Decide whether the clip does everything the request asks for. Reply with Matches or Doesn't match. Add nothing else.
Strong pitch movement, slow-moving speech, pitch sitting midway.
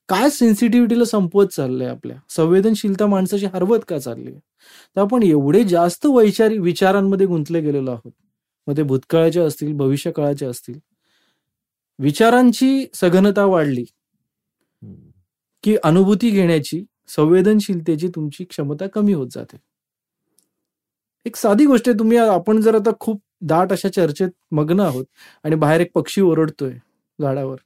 Matches